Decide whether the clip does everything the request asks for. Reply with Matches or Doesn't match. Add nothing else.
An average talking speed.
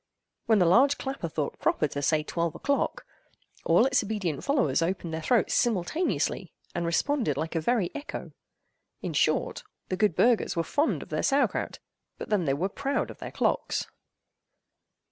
Matches